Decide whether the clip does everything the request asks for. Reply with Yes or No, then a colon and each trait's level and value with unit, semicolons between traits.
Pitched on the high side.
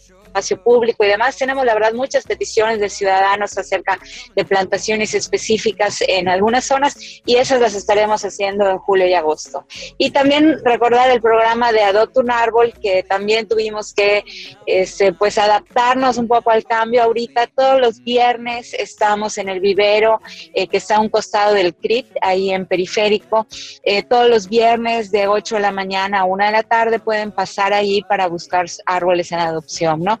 Yes: high, 210 Hz